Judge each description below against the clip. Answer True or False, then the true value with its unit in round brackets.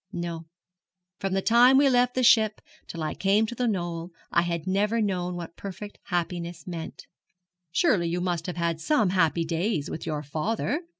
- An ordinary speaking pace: True (180 wpm)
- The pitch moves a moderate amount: True (4.4 semitones)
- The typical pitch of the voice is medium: True (180 Hz)